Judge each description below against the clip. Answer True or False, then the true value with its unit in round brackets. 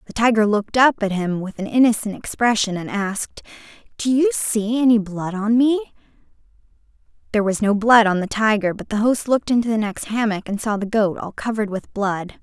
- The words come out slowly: False (205 wpm)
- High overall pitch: True (215 Hz)